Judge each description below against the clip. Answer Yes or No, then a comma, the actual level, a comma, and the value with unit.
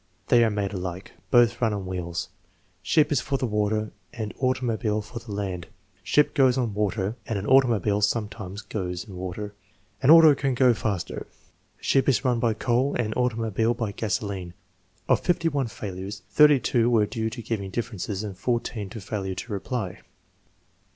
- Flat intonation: No, average, 3.6 semitones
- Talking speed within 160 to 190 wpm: Yes, average, 165 wpm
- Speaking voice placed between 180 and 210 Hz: No, low, 110 Hz